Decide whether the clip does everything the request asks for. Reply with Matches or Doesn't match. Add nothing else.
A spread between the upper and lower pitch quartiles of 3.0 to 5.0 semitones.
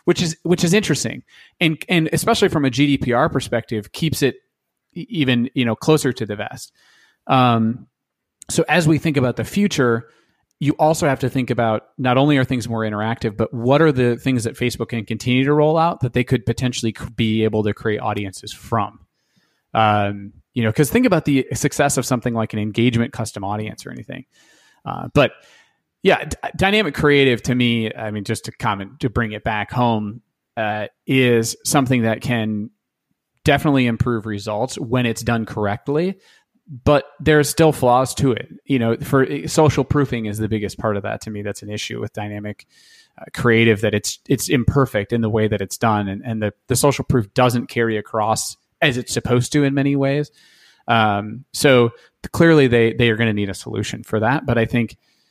Matches